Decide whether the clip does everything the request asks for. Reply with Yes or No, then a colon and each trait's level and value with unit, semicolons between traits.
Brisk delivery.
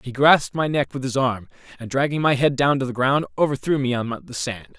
Yes: fast, 250 wpm